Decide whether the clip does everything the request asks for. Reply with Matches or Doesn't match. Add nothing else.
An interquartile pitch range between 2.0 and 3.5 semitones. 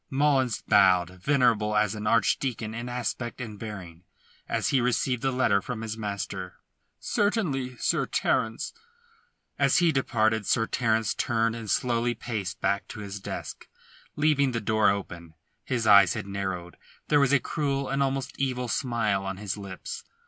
Doesn't match